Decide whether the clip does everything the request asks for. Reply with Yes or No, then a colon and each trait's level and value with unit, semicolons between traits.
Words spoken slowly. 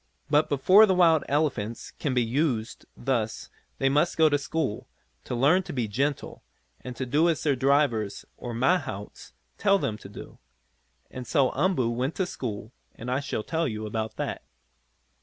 No: average, 175 wpm